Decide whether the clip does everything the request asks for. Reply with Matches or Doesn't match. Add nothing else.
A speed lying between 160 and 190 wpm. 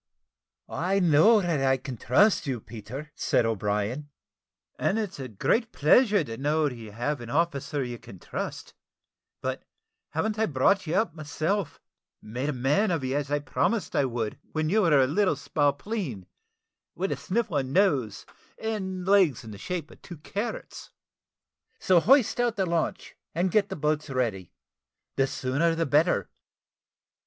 Matches